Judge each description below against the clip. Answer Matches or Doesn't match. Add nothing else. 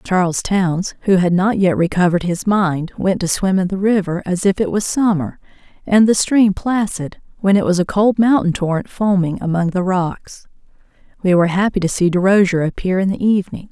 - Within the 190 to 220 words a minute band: Matches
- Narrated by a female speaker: Matches